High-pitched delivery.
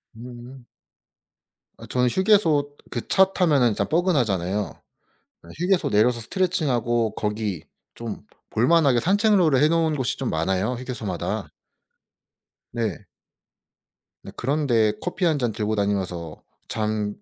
No: low, 120 Hz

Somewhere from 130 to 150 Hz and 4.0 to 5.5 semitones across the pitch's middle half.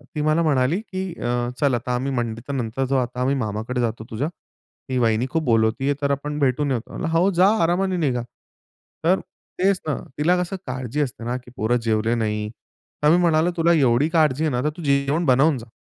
Yes: low, 135 Hz; average, 4.6 semitones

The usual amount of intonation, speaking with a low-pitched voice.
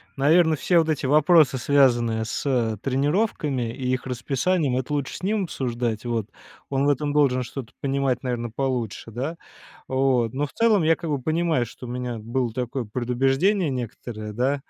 Yes: average, 3.5 semitones; low, 130 Hz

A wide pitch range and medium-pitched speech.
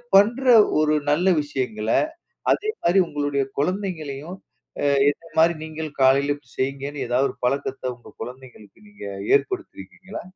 No: average, 4.3 semitones; medium, 145 Hz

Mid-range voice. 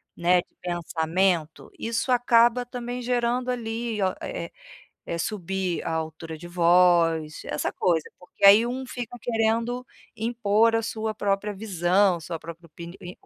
No: high, 200 Hz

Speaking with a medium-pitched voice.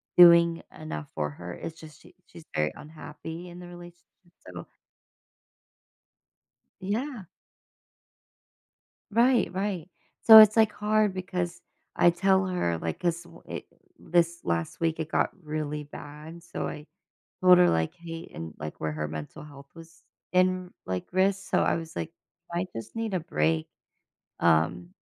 Yes: medium, 170 Hz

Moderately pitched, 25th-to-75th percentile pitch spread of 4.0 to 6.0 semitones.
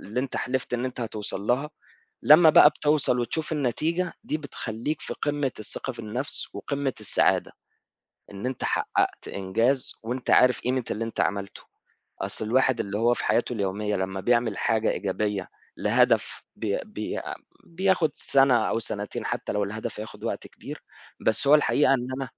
No: low, 120 Hz; average, 4.7 semitones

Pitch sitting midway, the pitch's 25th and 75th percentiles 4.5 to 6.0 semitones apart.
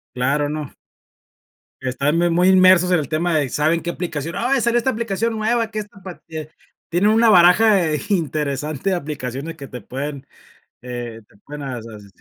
Yes: medium, 160 Hz; wide, 5.5 semitones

